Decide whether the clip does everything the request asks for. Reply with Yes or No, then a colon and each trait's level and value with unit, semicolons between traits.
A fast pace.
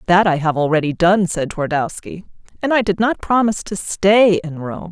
No: average, 195 wpm